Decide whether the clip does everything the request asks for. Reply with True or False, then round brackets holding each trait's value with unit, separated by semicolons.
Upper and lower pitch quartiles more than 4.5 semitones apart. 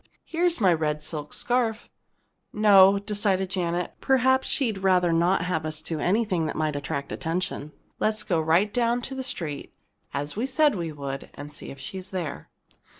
True (5.6 semitones)